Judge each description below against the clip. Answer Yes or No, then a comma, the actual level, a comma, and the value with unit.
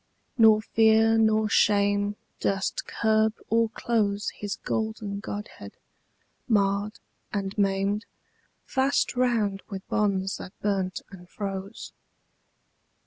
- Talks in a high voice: Yes, high, 205 Hz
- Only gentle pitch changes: Yes, narrow, 1.8 semitones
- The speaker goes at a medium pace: No, slow, 100 wpm